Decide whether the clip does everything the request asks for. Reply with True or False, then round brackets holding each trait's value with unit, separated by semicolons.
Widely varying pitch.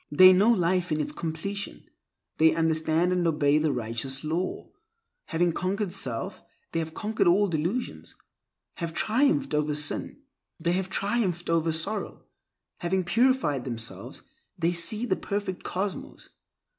False (4.0 semitones)